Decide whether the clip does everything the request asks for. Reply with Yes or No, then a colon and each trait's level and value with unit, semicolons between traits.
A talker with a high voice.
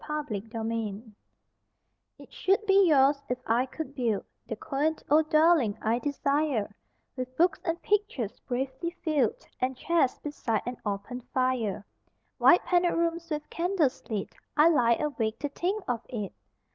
Yes: very high, 270 Hz